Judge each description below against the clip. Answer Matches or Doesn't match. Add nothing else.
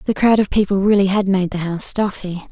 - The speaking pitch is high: Matches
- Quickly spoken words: Matches